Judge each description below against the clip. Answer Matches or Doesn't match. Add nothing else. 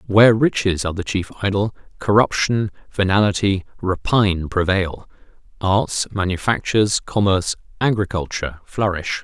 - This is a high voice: Doesn't match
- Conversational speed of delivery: Doesn't match